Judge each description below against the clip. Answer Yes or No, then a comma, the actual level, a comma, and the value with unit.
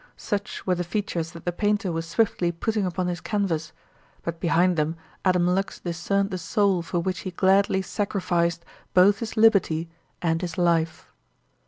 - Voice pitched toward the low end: No, medium, 180 Hz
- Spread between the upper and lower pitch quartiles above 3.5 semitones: No, average, 2.8 semitones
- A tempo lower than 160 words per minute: No, average, 165 wpm